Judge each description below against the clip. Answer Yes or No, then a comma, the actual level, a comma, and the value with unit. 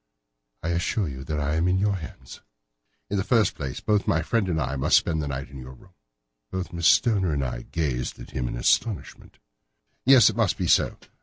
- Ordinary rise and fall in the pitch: No, wide, 5.8 semitones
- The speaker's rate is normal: No, fast, 215 wpm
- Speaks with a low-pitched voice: Yes, very low, 80 Hz